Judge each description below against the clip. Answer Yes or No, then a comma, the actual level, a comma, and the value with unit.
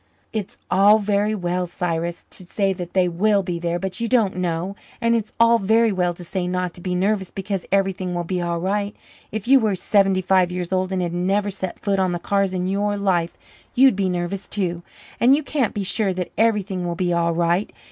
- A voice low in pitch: No, high, 190 Hz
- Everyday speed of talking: No, fast, 220 wpm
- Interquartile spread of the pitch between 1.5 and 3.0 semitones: Yes, narrow, 2.5 semitones